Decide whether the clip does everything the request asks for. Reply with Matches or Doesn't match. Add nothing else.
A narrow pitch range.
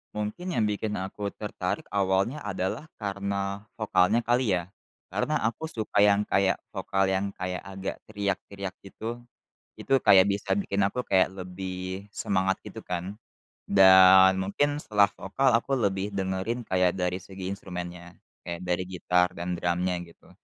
Matches